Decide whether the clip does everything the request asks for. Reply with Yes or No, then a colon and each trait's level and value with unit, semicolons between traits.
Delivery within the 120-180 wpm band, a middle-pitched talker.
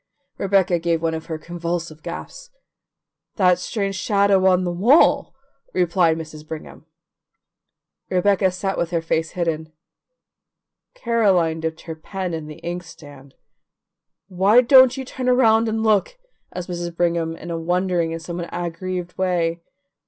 Yes: average, 140 wpm; medium, 175 Hz